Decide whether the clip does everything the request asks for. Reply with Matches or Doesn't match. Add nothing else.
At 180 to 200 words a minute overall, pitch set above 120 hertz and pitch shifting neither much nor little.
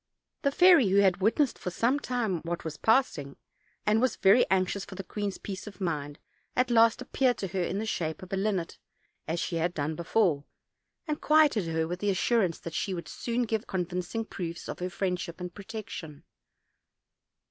Matches